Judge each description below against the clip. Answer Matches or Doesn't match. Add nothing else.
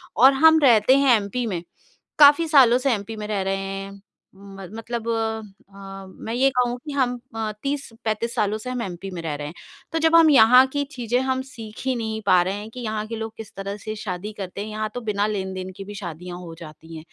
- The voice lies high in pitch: Matches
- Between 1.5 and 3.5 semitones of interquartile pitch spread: Doesn't match